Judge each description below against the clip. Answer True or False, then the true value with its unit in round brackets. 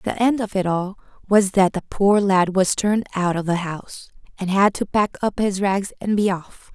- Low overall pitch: False (195 Hz)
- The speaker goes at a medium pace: False (230 wpm)